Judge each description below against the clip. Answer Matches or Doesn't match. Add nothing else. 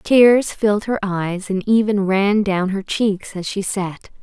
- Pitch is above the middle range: Matches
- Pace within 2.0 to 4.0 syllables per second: Matches